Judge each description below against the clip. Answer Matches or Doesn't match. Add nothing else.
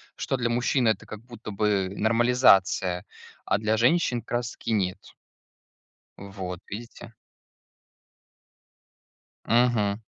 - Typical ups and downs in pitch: Matches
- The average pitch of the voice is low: Matches